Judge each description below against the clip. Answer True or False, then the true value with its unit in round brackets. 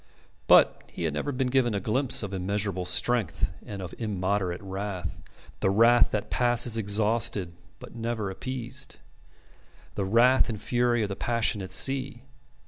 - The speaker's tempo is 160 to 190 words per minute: False (145 wpm)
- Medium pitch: False (110 Hz)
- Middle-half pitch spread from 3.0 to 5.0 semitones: True (3.8 semitones)